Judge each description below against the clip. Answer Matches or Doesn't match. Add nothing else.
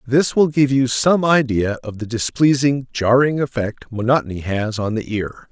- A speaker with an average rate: Matches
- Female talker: Doesn't match